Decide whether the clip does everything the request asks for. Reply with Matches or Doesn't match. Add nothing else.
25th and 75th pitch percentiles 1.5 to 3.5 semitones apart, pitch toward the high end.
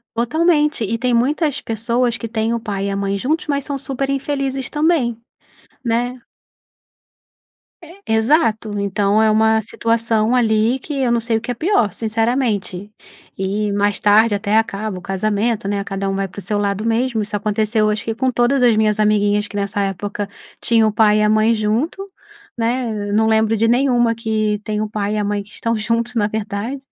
Matches